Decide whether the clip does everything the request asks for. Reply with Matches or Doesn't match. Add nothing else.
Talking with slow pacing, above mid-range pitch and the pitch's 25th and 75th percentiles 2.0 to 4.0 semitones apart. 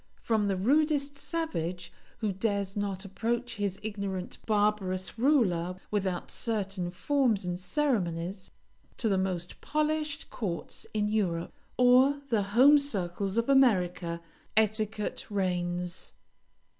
Doesn't match